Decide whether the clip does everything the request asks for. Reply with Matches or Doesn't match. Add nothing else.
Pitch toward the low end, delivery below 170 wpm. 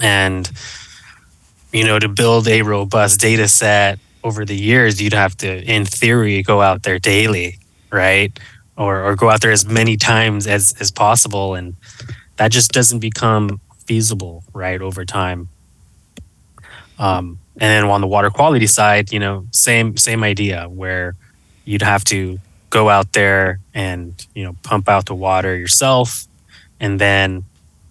Matches